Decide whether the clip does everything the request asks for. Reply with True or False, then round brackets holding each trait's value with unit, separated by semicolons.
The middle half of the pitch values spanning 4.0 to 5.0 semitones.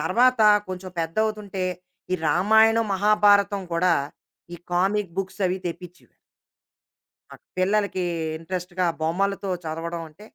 False (2.8 semitones)